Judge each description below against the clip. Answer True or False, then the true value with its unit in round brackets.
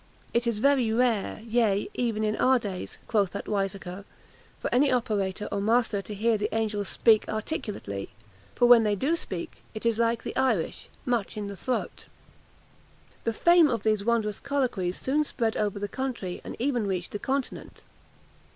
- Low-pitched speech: False (220 Hz)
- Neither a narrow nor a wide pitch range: True (3.3 semitones)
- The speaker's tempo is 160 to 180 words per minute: True (170 wpm)